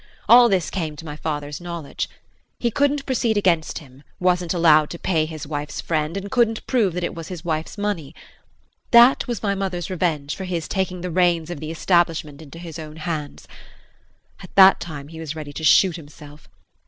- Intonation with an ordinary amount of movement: Yes, average, 3.5 semitones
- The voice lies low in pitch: No, medium, 170 Hz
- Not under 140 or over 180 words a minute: No, average, 190 wpm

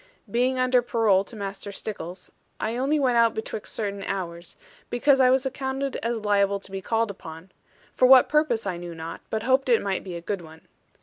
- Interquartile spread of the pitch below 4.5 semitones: No, average, 4.8 semitones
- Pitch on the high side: Yes, high, 220 Hz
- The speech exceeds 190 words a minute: Yes, average, 200 wpm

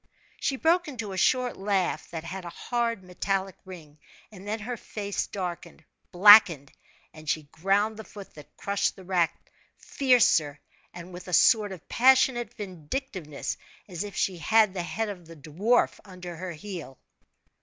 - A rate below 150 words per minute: No, average, 160 wpm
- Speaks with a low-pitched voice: No, high, 190 Hz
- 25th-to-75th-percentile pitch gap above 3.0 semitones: Yes, average, 4.1 semitones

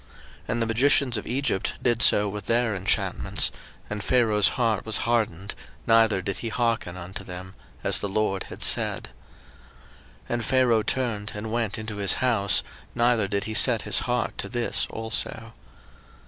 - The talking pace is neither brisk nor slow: Yes, average, 165 wpm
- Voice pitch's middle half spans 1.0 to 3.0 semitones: Yes, average, 2.7 semitones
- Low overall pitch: Yes, low, 110 Hz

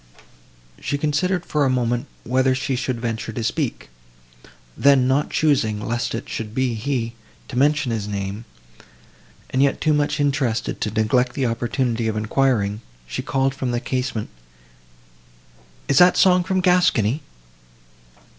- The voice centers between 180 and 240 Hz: No, low, 130 Hz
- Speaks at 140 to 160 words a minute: Yes, average, 145 wpm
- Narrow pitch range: No, average, 3.8 semitones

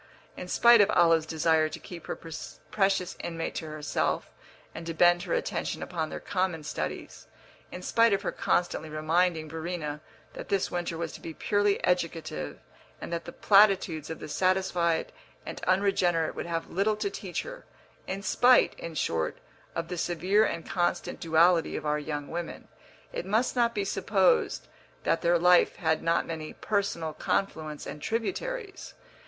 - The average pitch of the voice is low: No, medium, 170 Hz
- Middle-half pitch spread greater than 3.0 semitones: Yes, average, 3.5 semitones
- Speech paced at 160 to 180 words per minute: Yes, average, 165 wpm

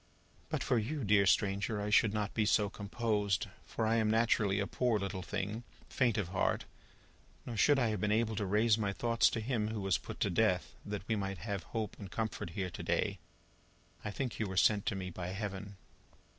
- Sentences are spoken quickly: Yes, fast, 210 wpm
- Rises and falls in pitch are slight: Yes, narrow, 2.2 semitones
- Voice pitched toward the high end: No, low, 105 Hz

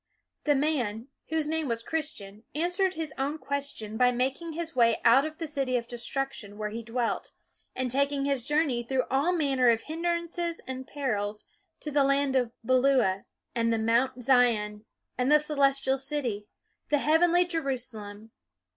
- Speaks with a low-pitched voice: No, very high, 270 Hz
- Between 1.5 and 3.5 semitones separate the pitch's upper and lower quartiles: No, average, 4.4 semitones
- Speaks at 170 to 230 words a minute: No, average, 160 wpm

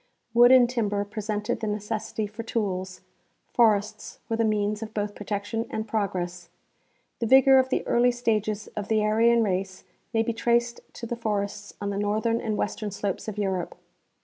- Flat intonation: Yes, narrow, 2.1 semitones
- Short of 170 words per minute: No, average, 175 wpm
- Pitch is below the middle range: No, high, 215 Hz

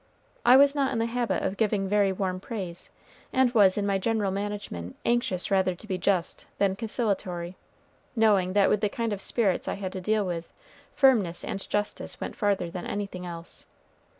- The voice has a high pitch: Yes, high, 200 Hz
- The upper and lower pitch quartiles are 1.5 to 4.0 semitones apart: Yes, average, 3.0 semitones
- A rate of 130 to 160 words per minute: No, average, 185 wpm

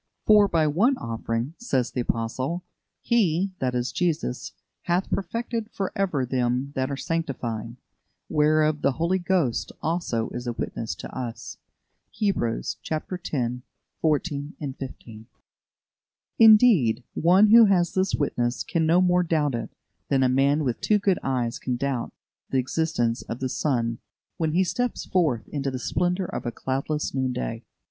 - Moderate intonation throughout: No, wide, 6.2 semitones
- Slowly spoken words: No, average, 150 wpm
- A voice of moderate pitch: Yes, medium, 145 Hz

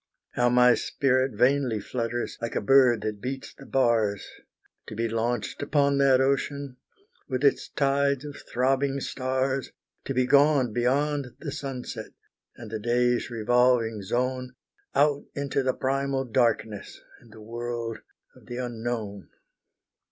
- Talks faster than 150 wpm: No, slow, 135 wpm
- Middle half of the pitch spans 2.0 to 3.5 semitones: Yes, average, 2.7 semitones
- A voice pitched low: Yes, low, 125 Hz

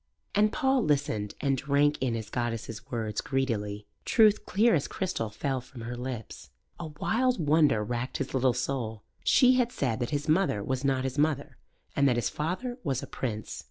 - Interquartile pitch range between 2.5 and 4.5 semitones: No, average, 5.1 semitones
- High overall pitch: No, low, 135 Hz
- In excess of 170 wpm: Yes, average, 185 wpm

